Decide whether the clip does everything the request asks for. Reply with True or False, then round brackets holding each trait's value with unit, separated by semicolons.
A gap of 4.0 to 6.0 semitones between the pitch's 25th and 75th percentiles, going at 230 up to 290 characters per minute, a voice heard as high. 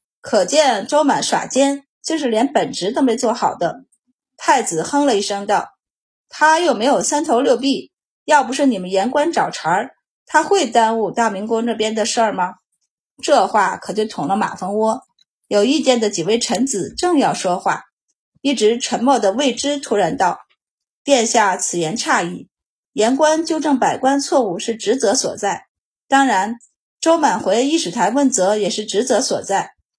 True (5.1 semitones; 240 characters per minute; 250 Hz)